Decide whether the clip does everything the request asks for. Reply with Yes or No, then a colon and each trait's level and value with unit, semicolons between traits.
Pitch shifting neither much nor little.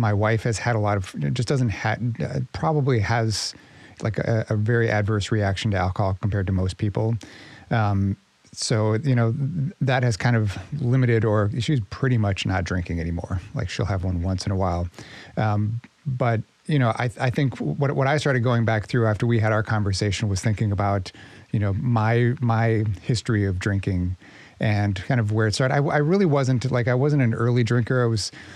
Yes: average, 3.5 semitones